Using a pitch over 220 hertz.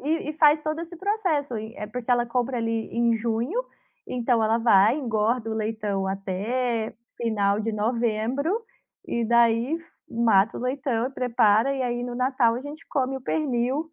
Yes: high, 240 Hz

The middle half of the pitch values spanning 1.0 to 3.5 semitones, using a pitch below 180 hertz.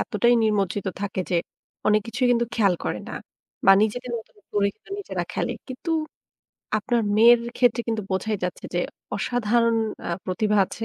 No: average, 2.9 semitones; high, 220 Hz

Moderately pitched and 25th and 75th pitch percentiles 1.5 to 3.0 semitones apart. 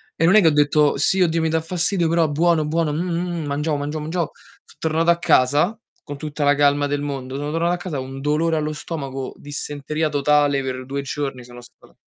Yes: medium, 150 Hz; narrow, 2.5 semitones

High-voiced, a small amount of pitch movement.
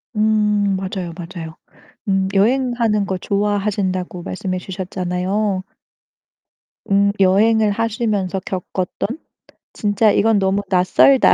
Yes: high, 200 Hz; narrow, 2.2 semitones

